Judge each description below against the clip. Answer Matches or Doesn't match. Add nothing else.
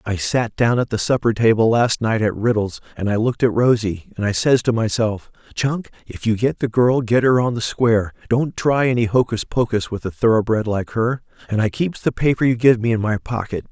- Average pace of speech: Doesn't match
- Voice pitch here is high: Doesn't match